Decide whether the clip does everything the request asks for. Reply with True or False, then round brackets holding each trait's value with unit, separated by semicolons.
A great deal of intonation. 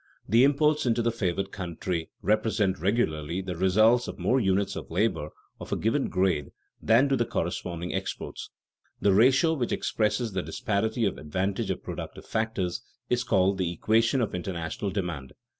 False (4.2 semitones)